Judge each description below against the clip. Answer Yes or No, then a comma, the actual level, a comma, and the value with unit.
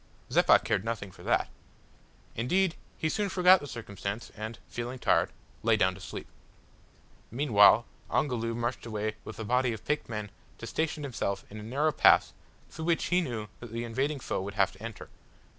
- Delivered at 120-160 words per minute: No, average, 180 wpm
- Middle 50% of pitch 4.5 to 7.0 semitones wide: Yes, average, 5.1 semitones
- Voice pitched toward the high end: No, low, 115 Hz